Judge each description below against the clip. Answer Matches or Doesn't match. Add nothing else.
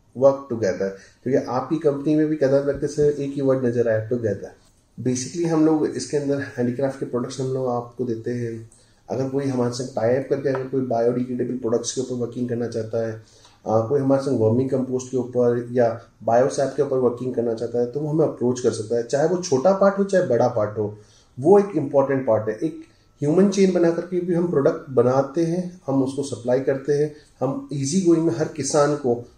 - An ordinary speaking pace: Doesn't match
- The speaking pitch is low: Matches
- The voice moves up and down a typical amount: Matches